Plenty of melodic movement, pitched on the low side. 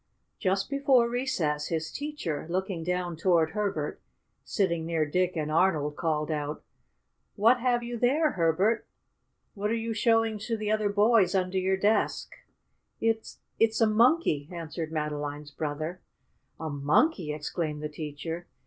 No: wide, 6.2 semitones; medium, 185 Hz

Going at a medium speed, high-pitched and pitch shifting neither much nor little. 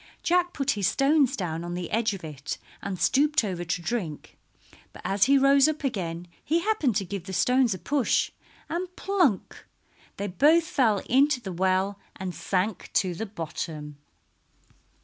No: average, 170 wpm; high, 205 Hz; wide, 7.7 semitones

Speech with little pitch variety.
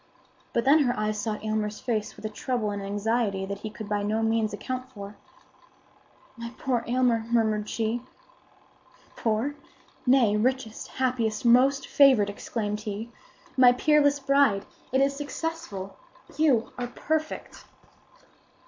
No: average, 3.6 semitones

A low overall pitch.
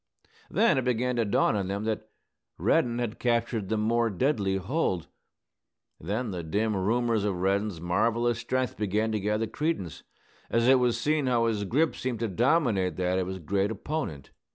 Yes: low, 110 Hz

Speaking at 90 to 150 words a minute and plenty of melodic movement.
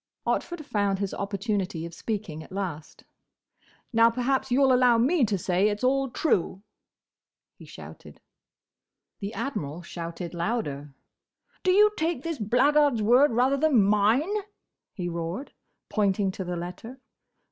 Yes: slow, 135 wpm; wide, 6.4 semitones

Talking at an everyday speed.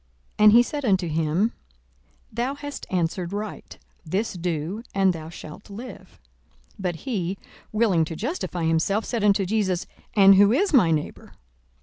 Yes: average, 155 wpm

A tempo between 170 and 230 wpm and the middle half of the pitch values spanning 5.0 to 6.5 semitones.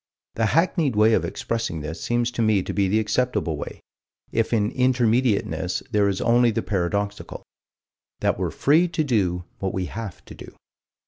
No: average, 175 wpm; average, 3.7 semitones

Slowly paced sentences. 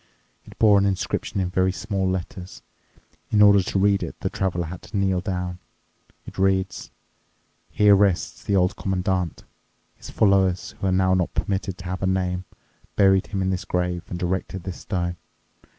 No: average, 175 wpm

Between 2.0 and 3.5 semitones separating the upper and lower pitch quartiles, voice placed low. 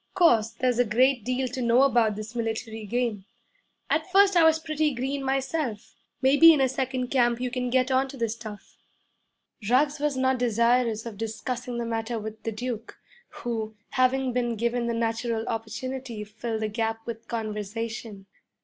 No: narrow, 2.6 semitones; high, 240 Hz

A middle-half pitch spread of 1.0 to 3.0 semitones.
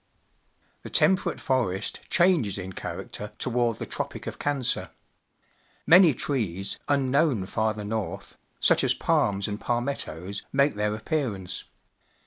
No: wide, 5.6 semitones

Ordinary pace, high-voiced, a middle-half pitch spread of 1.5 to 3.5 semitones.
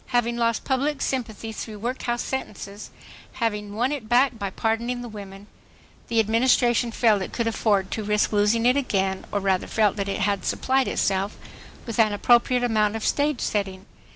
Yes: average, 175 wpm; high, 225 Hz; average, 2.9 semitones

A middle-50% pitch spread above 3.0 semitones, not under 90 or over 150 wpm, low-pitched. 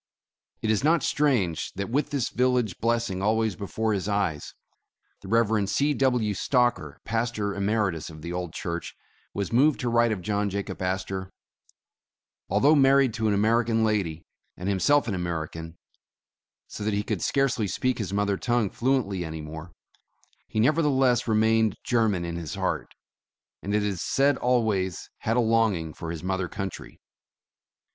No: average, 4.2 semitones; average, 165 wpm; low, 105 Hz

